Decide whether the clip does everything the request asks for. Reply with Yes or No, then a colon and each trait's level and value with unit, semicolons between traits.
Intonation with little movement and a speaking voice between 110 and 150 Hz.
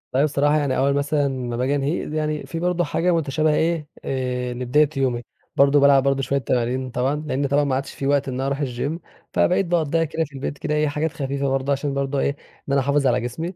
Yes: narrow, 2.2 semitones; medium, 140 Hz